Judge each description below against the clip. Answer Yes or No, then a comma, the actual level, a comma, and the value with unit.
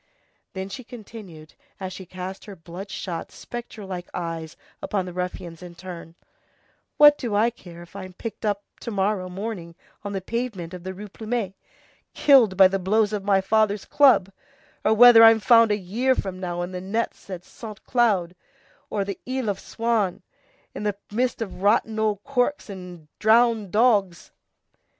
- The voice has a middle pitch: No, high, 200 Hz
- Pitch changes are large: No, average, 3.6 semitones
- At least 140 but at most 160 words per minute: No, average, 175 wpm